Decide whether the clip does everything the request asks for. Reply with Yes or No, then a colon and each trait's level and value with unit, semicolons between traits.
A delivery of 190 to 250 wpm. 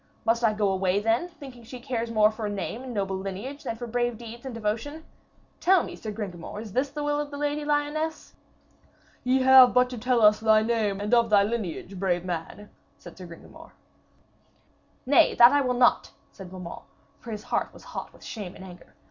Yes: fast, 205 wpm